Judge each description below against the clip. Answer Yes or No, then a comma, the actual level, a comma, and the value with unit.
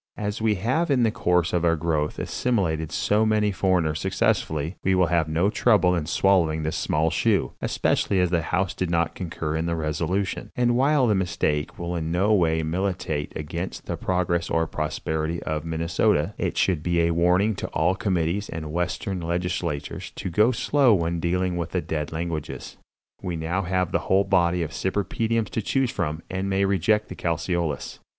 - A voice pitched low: Yes, very low, 90 Hz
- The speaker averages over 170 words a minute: Yes, average, 185 wpm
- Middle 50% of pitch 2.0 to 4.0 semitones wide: Yes, average, 3.2 semitones